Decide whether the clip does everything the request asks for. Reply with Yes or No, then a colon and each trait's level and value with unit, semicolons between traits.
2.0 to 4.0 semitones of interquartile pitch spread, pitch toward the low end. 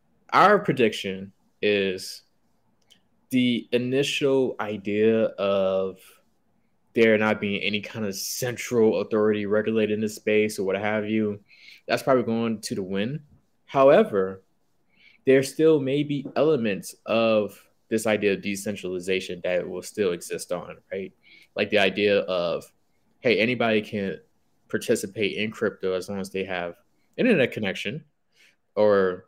Yes: average, 2.8 semitones; low, 105 Hz